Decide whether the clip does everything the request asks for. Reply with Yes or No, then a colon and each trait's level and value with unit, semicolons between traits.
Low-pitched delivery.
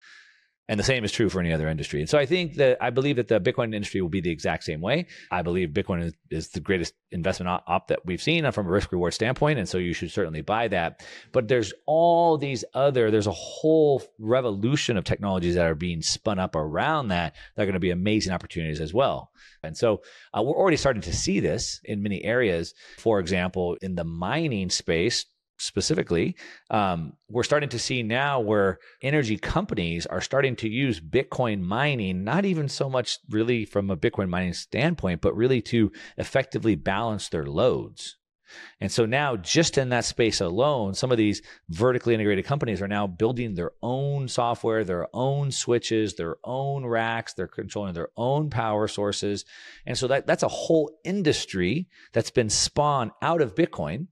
Yes: low, 110 Hz